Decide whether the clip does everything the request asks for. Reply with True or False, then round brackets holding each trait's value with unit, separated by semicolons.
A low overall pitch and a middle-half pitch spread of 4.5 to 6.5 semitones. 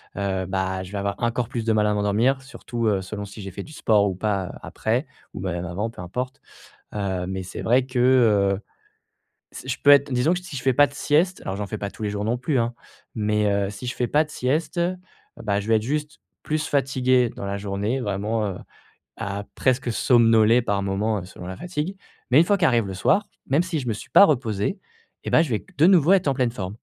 True (115 Hz; 5.0 semitones)